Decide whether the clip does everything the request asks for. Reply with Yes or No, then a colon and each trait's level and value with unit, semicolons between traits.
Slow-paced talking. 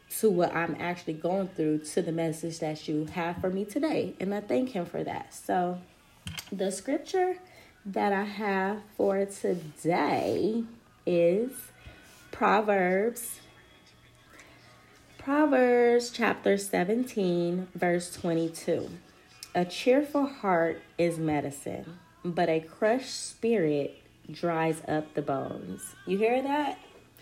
Yes: slow, 115 wpm